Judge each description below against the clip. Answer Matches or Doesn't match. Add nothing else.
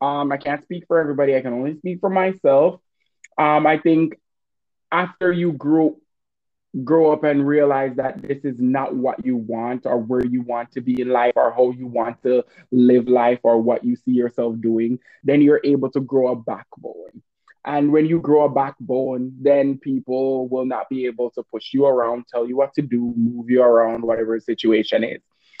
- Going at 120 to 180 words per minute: Doesn't match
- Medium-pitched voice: Doesn't match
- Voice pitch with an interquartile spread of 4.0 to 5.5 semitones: Doesn't match